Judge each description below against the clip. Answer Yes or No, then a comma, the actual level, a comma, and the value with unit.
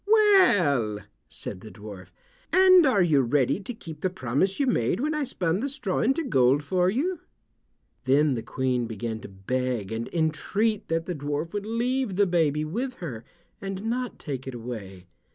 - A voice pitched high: No, medium, 165 Hz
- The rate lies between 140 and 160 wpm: No, average, 175 wpm